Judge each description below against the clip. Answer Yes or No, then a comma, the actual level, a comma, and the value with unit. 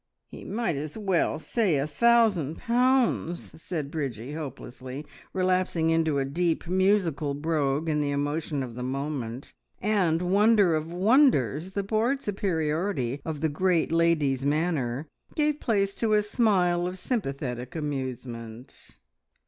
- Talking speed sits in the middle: No, slow, 130 wpm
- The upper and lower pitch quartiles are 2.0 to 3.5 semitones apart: No, wide, 5.6 semitones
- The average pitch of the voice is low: No, medium, 160 Hz